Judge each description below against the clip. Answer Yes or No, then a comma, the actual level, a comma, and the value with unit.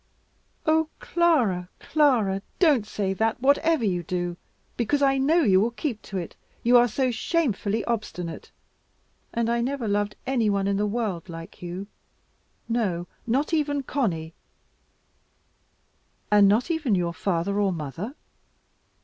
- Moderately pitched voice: No, high, 220 Hz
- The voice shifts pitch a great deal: Yes, wide, 5.9 semitones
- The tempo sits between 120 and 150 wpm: Yes, average, 140 wpm